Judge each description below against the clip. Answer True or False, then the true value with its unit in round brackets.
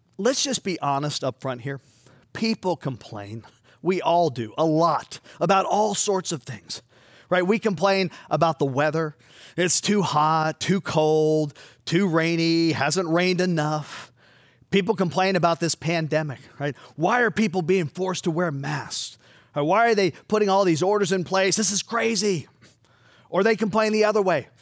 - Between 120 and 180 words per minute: True (165 wpm)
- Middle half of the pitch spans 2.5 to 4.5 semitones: False (4.9 semitones)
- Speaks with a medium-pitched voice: True (170 Hz)